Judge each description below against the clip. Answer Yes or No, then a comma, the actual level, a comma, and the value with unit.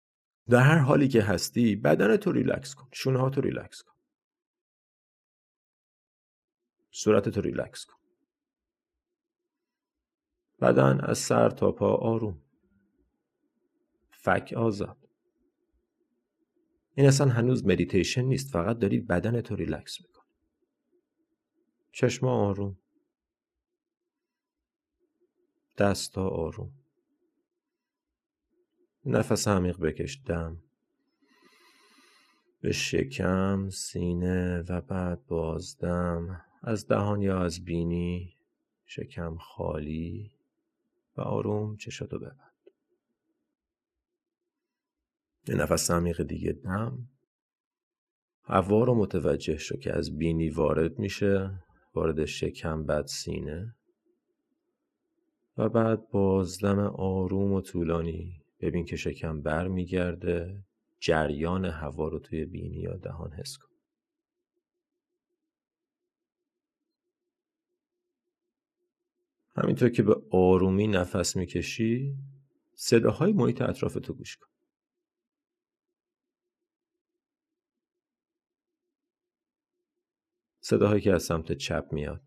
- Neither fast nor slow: No, slow, 85 wpm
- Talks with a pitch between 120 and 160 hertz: Yes, low, 135 Hz